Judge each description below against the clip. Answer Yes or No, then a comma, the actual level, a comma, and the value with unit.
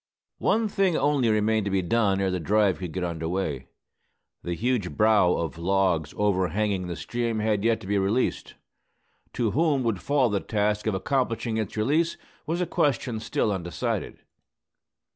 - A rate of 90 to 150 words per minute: No, average, 170 wpm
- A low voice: Yes, low, 105 Hz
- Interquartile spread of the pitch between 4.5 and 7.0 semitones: No, average, 4.0 semitones